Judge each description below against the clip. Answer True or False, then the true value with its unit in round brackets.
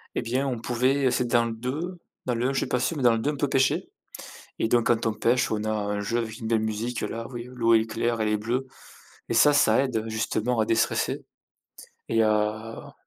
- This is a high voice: False (115 Hz)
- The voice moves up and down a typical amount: False (2.3 semitones)